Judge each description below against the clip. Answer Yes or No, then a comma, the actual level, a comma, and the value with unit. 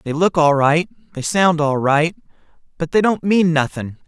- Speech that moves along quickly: No, average, 190 wpm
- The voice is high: No, medium, 160 Hz